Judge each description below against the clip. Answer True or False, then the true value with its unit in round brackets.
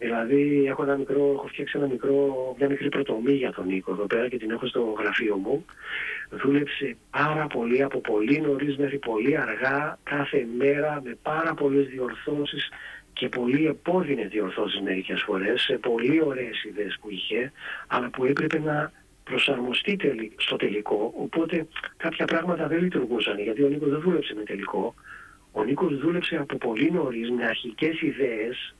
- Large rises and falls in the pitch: False (3.2 semitones)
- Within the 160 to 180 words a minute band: True (165 wpm)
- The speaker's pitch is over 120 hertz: True (140 Hz)